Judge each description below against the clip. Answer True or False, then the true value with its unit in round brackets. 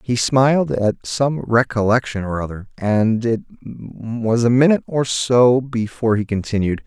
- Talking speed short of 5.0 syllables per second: True (4.4 syllables/s)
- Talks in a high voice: False (120 Hz)